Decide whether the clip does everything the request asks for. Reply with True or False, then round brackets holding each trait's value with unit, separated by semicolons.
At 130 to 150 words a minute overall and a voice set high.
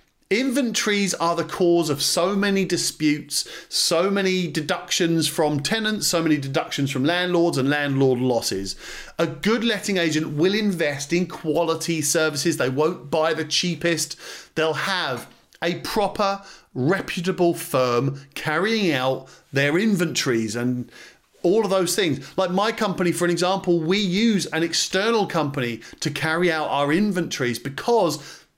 False (140 wpm; 170 Hz)